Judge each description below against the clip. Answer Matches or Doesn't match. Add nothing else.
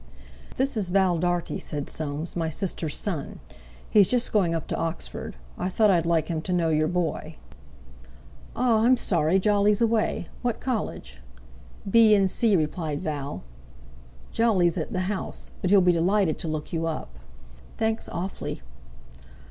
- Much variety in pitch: Doesn't match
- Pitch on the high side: Doesn't match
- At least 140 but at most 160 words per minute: Matches